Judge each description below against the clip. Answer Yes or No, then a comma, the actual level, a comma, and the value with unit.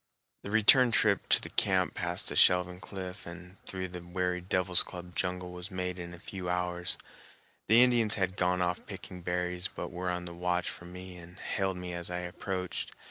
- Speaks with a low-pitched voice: Yes, very low, 90 Hz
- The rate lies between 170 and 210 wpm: Yes, average, 195 wpm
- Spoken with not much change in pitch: Yes, narrow, 0.9 semitones